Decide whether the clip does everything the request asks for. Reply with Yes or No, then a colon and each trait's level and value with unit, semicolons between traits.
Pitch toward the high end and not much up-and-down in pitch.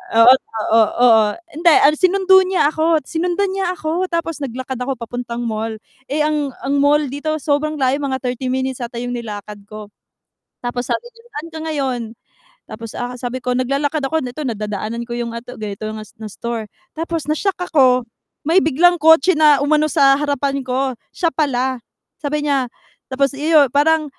No: very high, 275 Hz; average, 4.2 semitones